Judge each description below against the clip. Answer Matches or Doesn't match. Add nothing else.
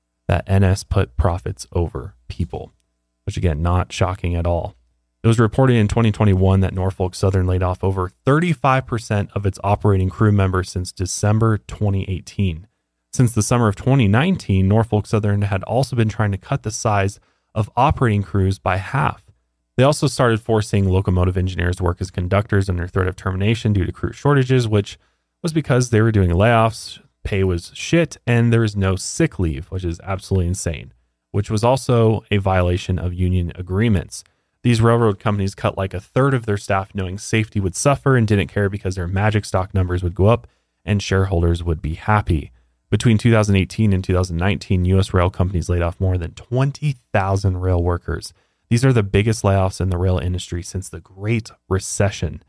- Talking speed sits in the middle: Matches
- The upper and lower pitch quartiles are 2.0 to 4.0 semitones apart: Matches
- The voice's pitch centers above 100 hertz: Doesn't match